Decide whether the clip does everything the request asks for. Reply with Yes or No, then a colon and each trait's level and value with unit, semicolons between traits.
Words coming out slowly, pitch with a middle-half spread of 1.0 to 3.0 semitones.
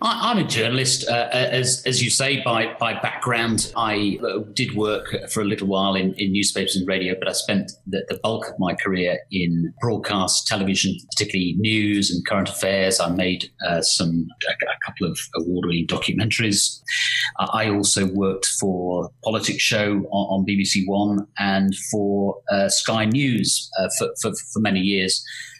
No: average, 165 wpm; narrow, 2.6 semitones